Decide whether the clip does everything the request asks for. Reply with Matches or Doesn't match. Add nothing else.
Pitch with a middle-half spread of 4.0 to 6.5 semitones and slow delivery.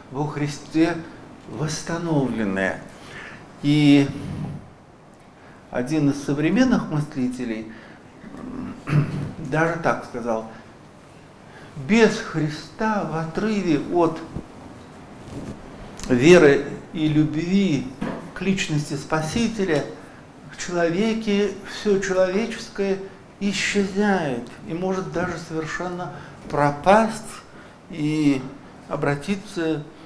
Matches